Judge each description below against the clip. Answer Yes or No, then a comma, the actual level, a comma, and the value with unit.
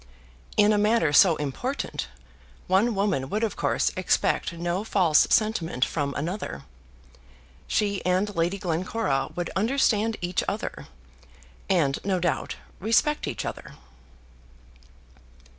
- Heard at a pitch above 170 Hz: Yes, medium, 185 Hz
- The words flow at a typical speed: No, slow, 115 wpm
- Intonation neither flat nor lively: Yes, average, 4.4 semitones